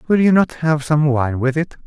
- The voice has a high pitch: No, medium, 150 Hz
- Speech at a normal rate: No, fast, 255 wpm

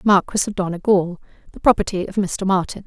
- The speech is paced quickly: No, average, 170 wpm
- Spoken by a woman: Yes, female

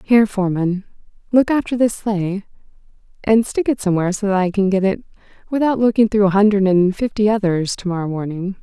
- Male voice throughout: No, female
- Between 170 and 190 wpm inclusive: Yes, average, 180 wpm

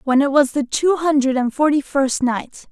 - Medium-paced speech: No, fast, 220 wpm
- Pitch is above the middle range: Yes, very high, 275 Hz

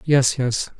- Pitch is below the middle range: Yes, low, 130 Hz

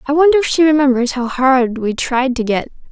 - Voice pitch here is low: No, very high, 270 Hz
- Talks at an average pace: No, fast, 225 wpm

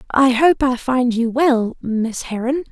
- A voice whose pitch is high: Yes, very high, 250 Hz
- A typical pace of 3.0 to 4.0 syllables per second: Yes, 3.8 syllables/s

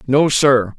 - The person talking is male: Yes, male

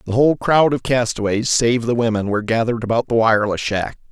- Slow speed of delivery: No, fast, 205 wpm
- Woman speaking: No, male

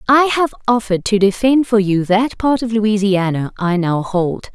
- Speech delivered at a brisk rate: No, average, 185 wpm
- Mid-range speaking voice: No, high, 210 Hz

